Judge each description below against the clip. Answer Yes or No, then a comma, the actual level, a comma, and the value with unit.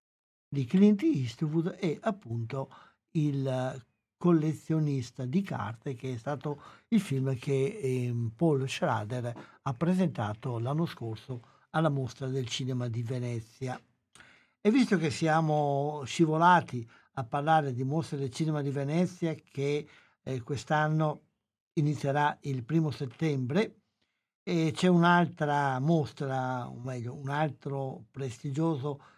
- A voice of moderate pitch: Yes, medium, 145 Hz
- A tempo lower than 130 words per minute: Yes, slow, 115 wpm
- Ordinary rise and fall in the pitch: Yes, average, 3.5 semitones